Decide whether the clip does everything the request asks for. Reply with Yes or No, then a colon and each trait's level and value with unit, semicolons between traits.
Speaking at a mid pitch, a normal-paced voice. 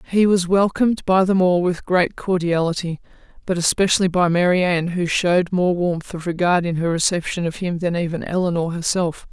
Yes: medium, 175 Hz; average, 180 wpm